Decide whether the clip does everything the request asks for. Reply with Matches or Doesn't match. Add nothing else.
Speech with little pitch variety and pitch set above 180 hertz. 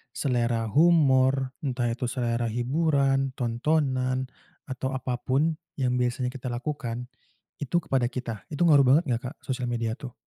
Doesn't match